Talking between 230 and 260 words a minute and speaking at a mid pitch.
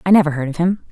No: fast, 330 wpm; medium, 165 Hz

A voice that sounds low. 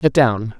Yes: low, 125 Hz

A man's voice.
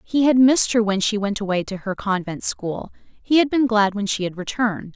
No: female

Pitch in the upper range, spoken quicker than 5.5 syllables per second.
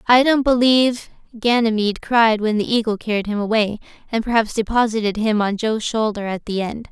Yes: high, 220 Hz; 5.7 syllables/s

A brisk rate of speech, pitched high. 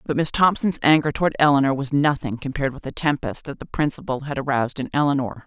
No: fast, 210 wpm; medium, 140 Hz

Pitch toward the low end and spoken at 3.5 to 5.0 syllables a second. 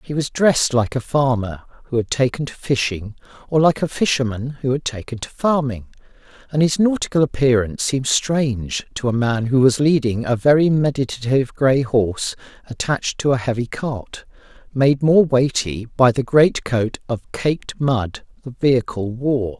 Yes: low, 130 Hz; 4.9 syllables/s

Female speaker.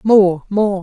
Yes: female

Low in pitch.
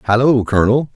Yes: low, 120 Hz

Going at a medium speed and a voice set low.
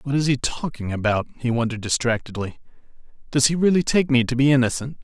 Yes: average, 190 wpm; low, 130 Hz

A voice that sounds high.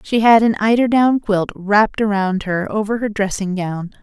Yes: high, 210 Hz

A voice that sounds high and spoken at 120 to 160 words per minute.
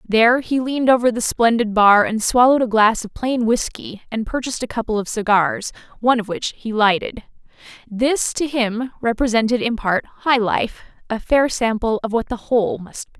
No: high, 225 Hz; average, 185 wpm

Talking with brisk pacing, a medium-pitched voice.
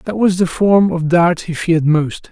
Yes: fast, 235 wpm; medium, 175 Hz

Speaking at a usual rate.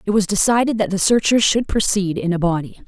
No: fast, 230 wpm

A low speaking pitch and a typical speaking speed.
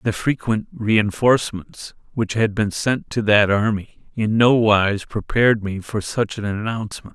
Yes: low, 110 Hz; average, 150 wpm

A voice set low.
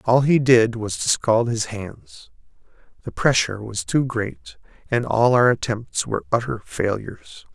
Yes: low, 110 Hz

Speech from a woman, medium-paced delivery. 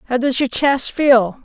No: female; fast, 210 wpm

